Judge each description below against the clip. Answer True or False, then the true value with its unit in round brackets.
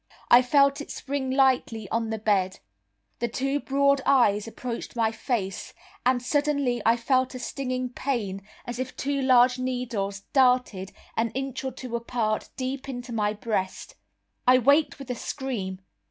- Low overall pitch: False (250 Hz)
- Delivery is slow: False (155 wpm)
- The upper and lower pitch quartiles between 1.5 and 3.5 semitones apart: True (2.9 semitones)